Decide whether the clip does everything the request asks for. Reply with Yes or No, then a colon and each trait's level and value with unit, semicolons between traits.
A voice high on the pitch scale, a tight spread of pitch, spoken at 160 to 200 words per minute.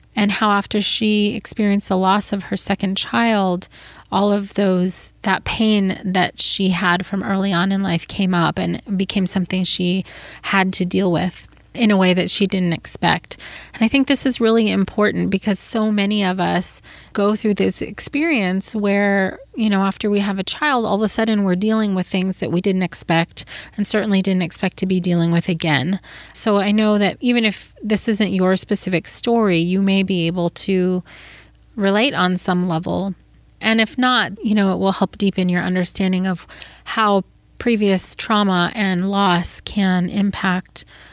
Yes: high, 195 Hz; narrow, 2.3 semitones; average, 180 wpm